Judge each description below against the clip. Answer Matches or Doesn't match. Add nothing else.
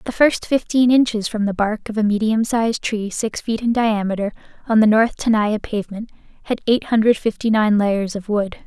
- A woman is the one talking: Matches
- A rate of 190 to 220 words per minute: Matches